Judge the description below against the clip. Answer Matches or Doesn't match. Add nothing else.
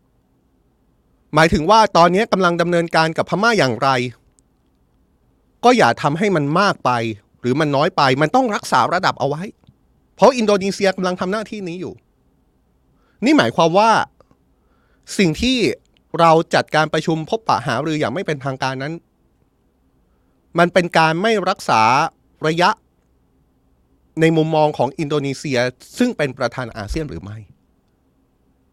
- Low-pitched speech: Doesn't match